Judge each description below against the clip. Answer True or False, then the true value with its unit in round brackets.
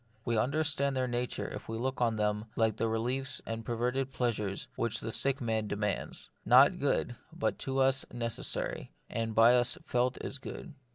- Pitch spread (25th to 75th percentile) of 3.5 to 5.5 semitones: False (2.7 semitones)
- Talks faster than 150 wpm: True (180 wpm)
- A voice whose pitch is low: True (120 Hz)